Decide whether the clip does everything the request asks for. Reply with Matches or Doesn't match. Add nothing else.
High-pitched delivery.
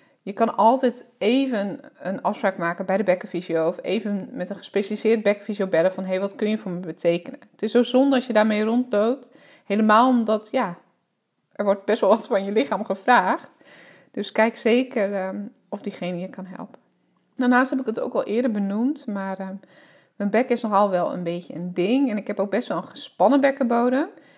Matches